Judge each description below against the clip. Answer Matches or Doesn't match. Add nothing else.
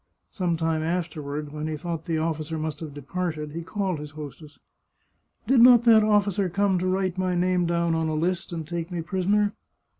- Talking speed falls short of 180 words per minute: Doesn't match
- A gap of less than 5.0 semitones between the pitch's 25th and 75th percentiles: Matches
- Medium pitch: Matches